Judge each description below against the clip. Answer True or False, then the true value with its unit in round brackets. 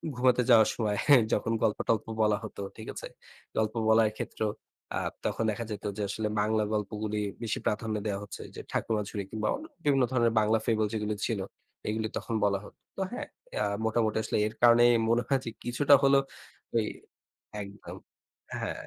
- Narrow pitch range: True (1.8 semitones)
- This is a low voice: True (110 Hz)